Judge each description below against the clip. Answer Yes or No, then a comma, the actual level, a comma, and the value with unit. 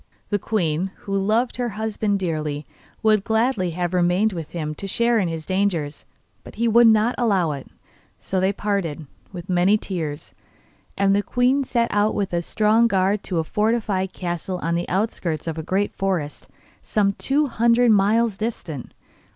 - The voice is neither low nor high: No, high, 195 Hz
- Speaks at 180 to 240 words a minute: No, average, 165 wpm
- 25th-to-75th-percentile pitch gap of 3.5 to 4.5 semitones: Yes, average, 4.1 semitones